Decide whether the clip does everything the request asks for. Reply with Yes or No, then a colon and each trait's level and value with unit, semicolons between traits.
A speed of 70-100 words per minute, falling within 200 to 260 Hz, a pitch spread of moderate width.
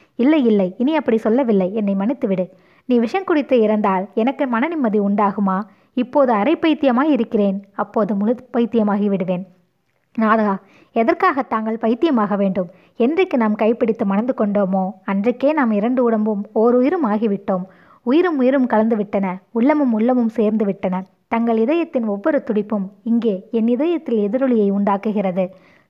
No: average, 125 wpm; high, 225 Hz; average, 4.0 semitones